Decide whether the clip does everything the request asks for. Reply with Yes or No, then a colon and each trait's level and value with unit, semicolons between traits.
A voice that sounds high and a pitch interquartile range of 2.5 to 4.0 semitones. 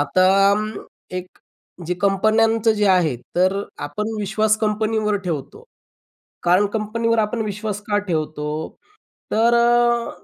Yes: high, 210 Hz; average, 3.3 semitones